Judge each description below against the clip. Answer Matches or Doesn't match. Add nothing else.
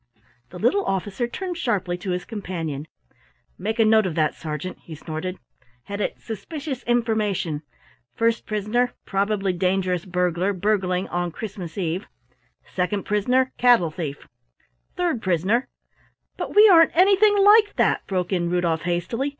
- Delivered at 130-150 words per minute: Matches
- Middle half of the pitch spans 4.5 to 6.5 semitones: Matches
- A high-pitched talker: Matches